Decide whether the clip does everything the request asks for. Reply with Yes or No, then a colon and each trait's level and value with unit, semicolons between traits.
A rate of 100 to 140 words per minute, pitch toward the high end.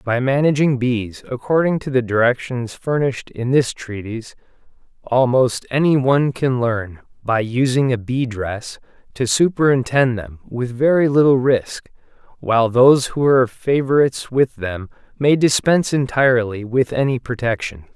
No: slow, 135 wpm; low, 125 Hz